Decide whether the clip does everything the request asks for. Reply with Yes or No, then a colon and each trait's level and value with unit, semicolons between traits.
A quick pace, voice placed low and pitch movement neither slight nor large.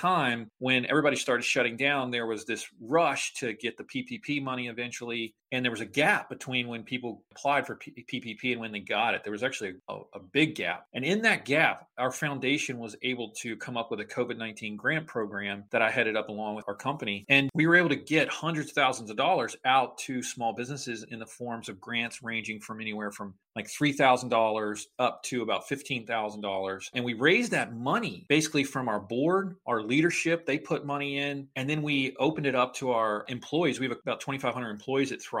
Yes: fast, 210 wpm; low, 125 Hz; average, 4.1 semitones